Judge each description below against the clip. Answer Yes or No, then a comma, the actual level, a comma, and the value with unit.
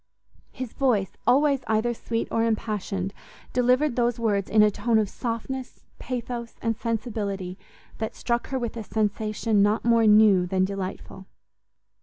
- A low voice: No, high, 225 Hz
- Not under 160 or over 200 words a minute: No, average, 145 wpm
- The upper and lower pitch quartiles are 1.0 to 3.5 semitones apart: Yes, narrow, 2.6 semitones